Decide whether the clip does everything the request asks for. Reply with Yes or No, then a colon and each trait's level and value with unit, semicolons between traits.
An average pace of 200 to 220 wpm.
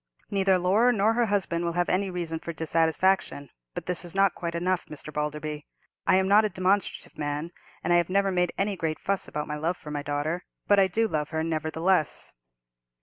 Yes: fast, 205 wpm